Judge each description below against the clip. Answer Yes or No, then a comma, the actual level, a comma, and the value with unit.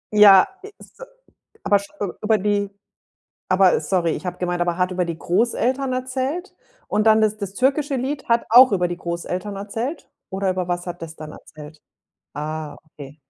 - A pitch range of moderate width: Yes, average, 5.0 semitones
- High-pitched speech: Yes, high, 195 Hz